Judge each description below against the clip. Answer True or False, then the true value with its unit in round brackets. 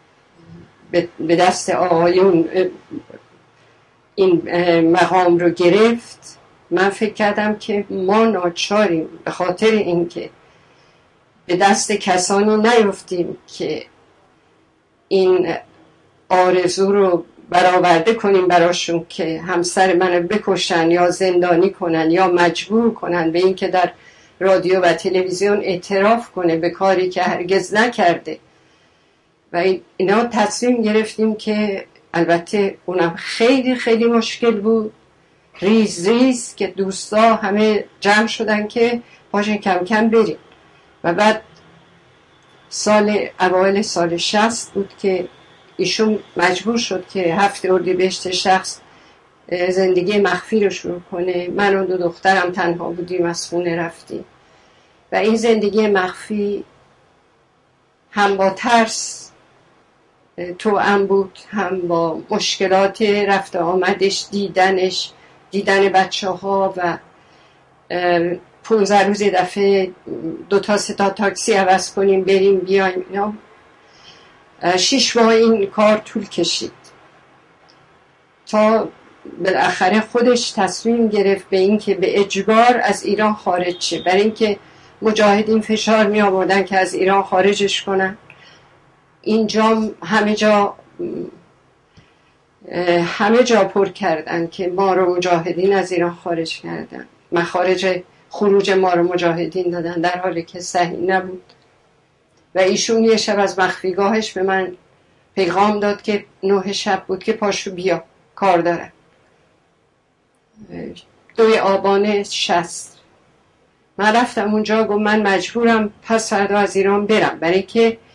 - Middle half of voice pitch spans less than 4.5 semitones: True (2.9 semitones)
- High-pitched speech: True (195 Hz)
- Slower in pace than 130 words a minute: True (115 wpm)